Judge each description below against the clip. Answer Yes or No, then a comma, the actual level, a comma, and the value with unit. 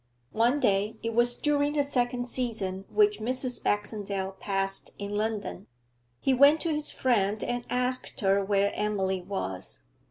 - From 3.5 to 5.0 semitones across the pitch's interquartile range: Yes, average, 4.4 semitones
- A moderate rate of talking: Yes, average, 150 wpm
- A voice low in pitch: No, high, 220 Hz